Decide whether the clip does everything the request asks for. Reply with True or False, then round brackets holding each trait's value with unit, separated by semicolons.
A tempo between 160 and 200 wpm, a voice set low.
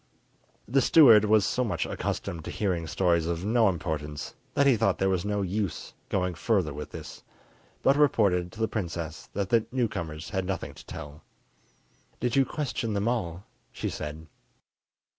True (165 wpm; 95 Hz)